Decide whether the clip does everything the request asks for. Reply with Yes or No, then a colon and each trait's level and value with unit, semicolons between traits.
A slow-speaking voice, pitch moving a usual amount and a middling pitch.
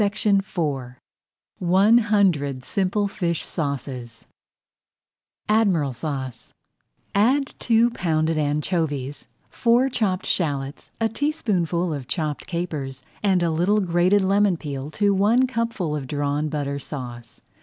No: slow, 115 wpm; wide, 6.1 semitones; medium, 170 Hz